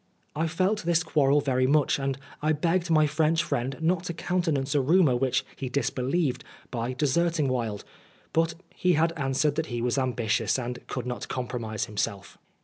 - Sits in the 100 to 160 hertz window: Yes, medium, 140 Hz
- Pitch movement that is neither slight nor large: Yes, average, 4.4 semitones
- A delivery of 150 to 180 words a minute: Yes, average, 175 wpm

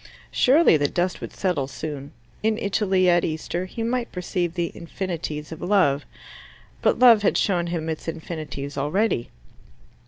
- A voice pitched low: No, medium, 175 Hz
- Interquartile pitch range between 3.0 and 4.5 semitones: Yes, average, 4.1 semitones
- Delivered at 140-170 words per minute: Yes, average, 150 wpm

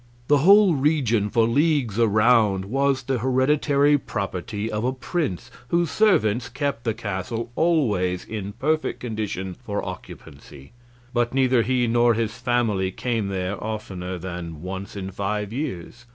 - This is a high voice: No, low, 115 Hz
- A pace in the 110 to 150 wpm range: Yes, average, 140 wpm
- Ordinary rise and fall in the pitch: Yes, average, 5.0 semitones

